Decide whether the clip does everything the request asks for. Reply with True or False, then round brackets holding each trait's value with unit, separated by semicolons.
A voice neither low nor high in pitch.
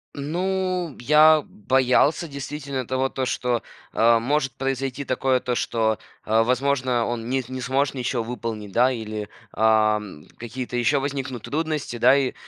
False (130 Hz)